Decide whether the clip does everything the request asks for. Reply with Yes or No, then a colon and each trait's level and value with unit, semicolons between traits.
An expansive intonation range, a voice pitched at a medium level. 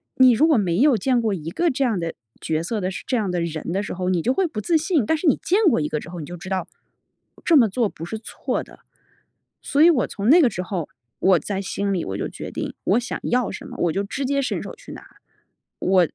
No: wide, 6.7 semitones; high, 210 Hz